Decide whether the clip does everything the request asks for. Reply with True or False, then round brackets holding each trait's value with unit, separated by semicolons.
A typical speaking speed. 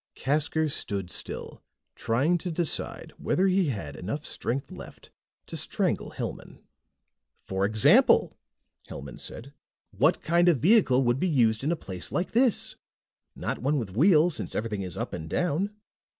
True (150 wpm)